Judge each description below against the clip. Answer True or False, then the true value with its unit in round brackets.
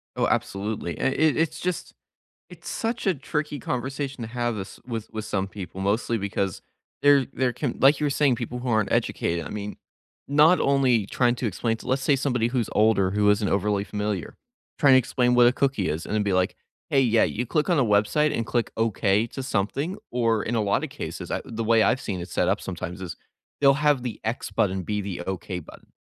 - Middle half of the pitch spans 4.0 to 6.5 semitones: True (4.8 semitones)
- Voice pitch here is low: True (115 Hz)